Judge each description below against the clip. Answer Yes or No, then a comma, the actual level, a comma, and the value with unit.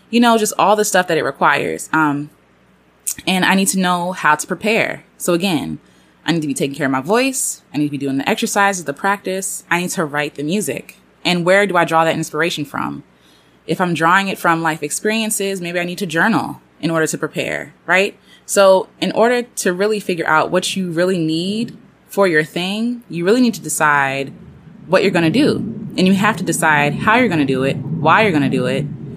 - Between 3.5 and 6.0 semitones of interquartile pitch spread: Yes, average, 4.7 semitones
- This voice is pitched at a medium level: Yes, medium, 175 Hz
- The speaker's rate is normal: No, fast, 225 wpm